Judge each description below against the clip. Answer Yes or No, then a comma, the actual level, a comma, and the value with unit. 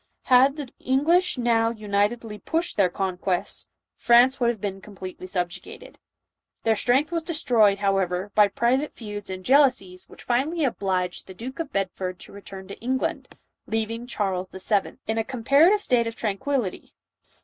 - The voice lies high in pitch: Yes, high, 225 Hz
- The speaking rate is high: No, average, 155 wpm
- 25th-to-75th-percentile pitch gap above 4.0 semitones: Yes, average, 5.1 semitones